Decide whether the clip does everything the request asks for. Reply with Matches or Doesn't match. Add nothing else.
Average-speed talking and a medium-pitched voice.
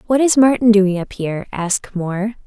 Doesn't match